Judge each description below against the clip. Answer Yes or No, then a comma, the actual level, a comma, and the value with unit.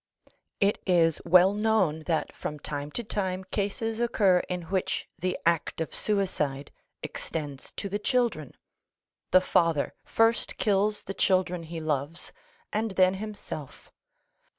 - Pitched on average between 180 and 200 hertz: Yes, medium, 185 Hz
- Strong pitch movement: No, average, 4.1 semitones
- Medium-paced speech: No, slow, 130 wpm